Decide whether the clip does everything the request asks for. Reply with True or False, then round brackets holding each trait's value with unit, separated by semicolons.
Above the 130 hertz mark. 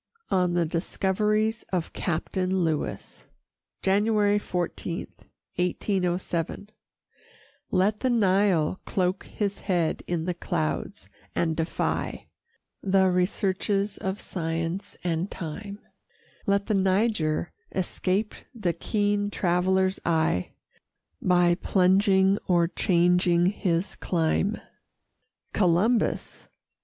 True (185 Hz)